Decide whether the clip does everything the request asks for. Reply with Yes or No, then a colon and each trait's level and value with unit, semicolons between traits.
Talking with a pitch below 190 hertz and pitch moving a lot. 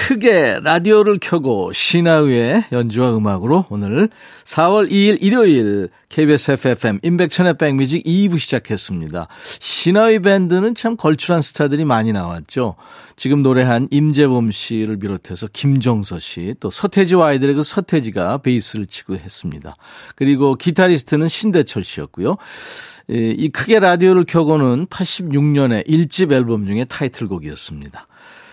Yes: medium, 140 Hz; wide, 7.7 semitones